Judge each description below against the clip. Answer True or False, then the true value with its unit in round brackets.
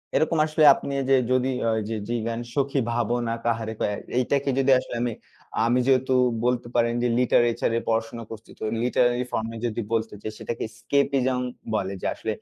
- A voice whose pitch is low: True (120 Hz)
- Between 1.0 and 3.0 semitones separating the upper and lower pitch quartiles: True (2.4 semitones)